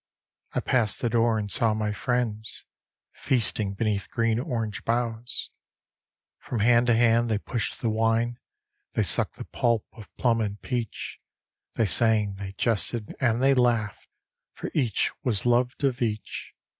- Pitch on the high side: No, low, 115 Hz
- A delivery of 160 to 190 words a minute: No, average, 150 wpm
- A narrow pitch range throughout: Yes, narrow, 2.0 semitones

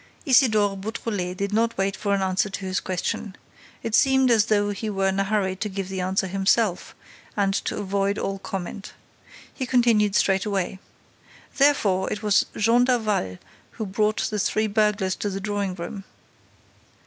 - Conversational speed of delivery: Yes, average, 165 wpm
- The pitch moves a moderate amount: No, narrow, 2.0 semitones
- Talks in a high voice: Yes, high, 200 Hz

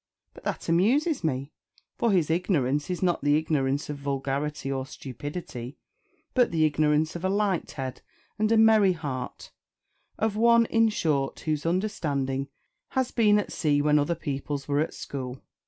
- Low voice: No, medium, 155 Hz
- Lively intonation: Yes, wide, 6.0 semitones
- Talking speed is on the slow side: No, average, 160 wpm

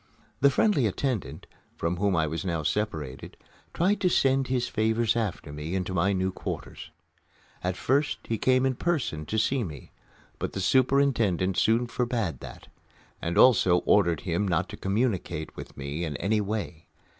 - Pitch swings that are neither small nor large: No, wide, 6.5 semitones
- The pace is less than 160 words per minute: No, average, 165 wpm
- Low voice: Yes, low, 100 Hz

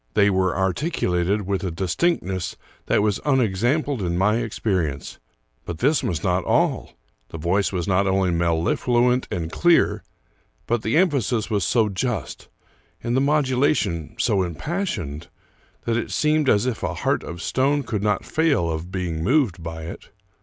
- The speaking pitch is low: Yes, low, 100 Hz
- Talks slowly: No, average, 165 wpm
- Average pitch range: No, wide, 6.5 semitones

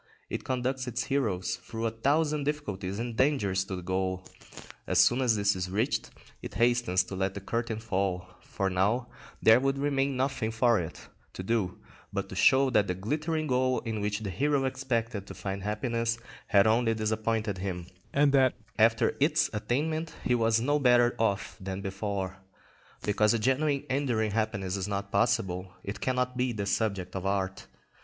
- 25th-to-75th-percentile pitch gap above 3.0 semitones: Yes, average, 4.6 semitones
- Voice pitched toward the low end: Yes, low, 110 Hz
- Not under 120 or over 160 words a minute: No, average, 175 wpm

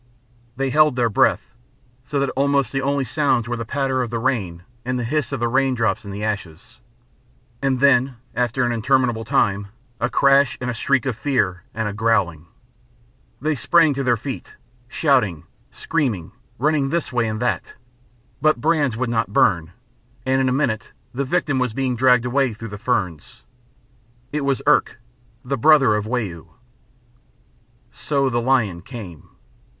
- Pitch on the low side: Yes, low, 125 Hz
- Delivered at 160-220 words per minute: Yes, average, 165 wpm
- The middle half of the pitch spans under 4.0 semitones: Yes, average, 3.6 semitones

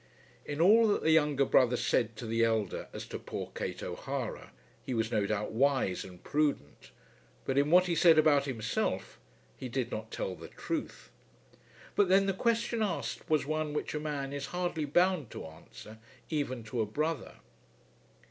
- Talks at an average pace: Yes, average, 175 wpm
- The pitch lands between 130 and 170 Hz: Yes, medium, 140 Hz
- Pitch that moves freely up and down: Yes, wide, 5.9 semitones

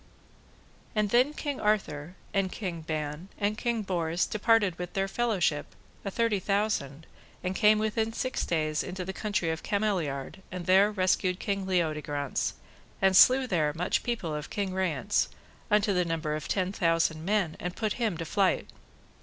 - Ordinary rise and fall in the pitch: Yes, average, 4.3 semitones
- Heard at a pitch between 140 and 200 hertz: Yes, high, 190 Hz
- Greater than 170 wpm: No, average, 160 wpm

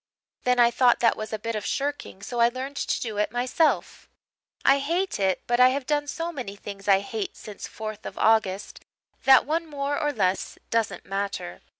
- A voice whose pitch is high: Yes, high, 240 Hz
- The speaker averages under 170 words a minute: No, average, 200 wpm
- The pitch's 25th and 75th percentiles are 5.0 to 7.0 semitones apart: Yes, average, 5.3 semitones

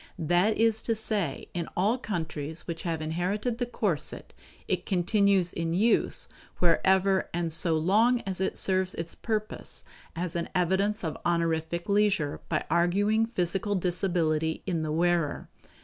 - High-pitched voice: No, medium, 180 Hz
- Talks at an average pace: Yes, average, 145 wpm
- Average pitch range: Yes, average, 3.6 semitones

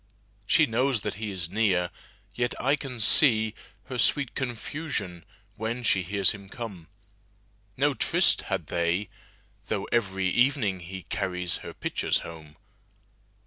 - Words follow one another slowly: Yes, slow, 120 wpm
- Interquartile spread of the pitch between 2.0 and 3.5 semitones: No, average, 4.2 semitones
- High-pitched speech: No, low, 105 Hz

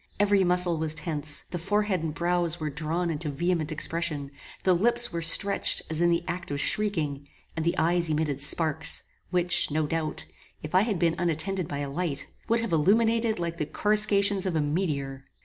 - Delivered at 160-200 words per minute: Yes, average, 185 wpm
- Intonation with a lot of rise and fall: No, average, 3.2 semitones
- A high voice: No, medium, 170 Hz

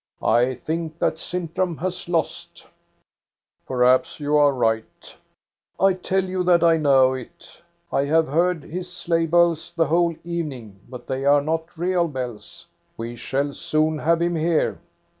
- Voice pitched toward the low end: No, medium, 160 Hz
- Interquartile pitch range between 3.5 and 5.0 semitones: Yes, average, 4.1 semitones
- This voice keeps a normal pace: Yes, average, 160 wpm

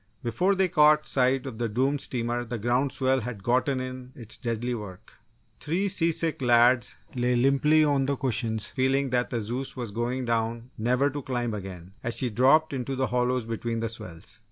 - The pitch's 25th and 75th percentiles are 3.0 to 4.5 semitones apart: No, narrow, 2.6 semitones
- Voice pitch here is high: No, low, 125 Hz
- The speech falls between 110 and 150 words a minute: No, average, 185 wpm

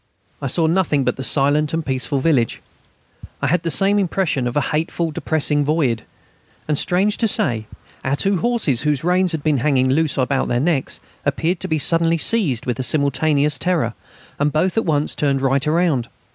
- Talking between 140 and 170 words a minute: No, average, 190 wpm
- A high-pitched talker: No, medium, 150 Hz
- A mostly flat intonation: No, average, 3.6 semitones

